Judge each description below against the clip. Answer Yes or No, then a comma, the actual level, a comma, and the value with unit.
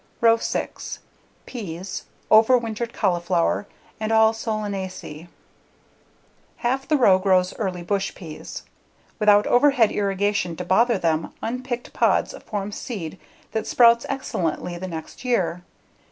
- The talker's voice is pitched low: No, high, 205 Hz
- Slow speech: Yes, slow, 115 wpm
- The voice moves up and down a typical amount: Yes, average, 4.2 semitones